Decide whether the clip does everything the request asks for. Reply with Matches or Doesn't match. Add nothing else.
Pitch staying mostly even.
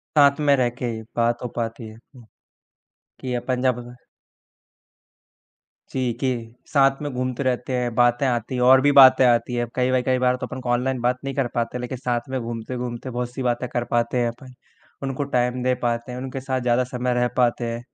Matches